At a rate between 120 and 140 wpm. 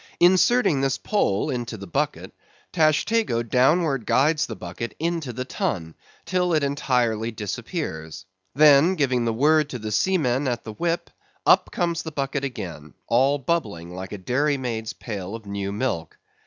No: average, 155 wpm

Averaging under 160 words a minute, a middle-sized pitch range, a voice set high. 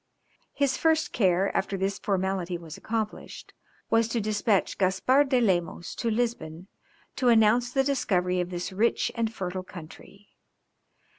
Yes: average, 140 wpm; average, 4.3 semitones; high, 200 Hz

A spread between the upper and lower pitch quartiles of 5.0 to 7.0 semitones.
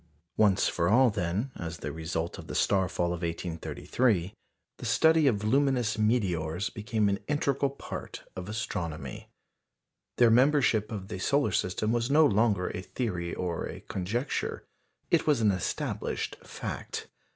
Yes: wide, 5.6 semitones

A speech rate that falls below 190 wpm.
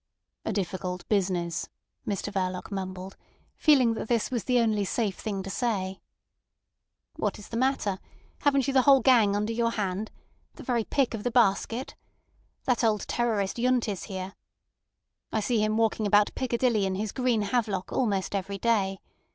Yes: average, 165 wpm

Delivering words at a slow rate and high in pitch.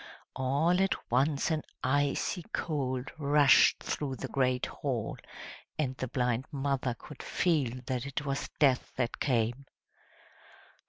No: slow, 125 wpm; low, 135 Hz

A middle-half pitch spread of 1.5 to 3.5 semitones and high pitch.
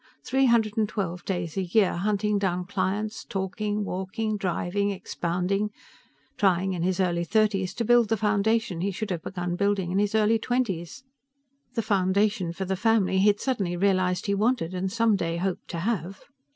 Yes: average, 2.8 semitones; high, 195 Hz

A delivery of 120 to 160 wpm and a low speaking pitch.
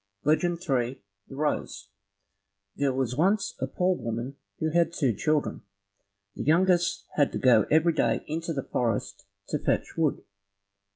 No: average, 150 wpm; medium, 150 Hz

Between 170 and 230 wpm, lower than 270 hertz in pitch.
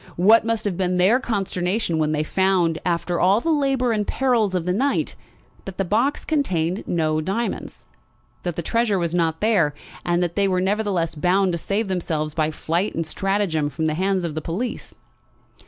Yes: average, 190 wpm; medium, 185 Hz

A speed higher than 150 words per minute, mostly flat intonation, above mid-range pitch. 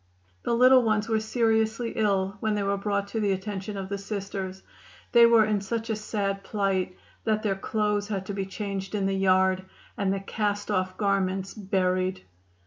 Yes: average, 185 wpm; narrow, 1.9 semitones; high, 200 Hz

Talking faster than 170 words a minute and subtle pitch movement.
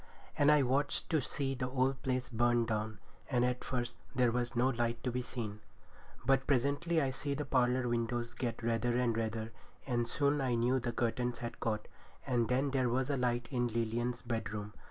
Yes: average, 195 wpm; narrow, 2.0 semitones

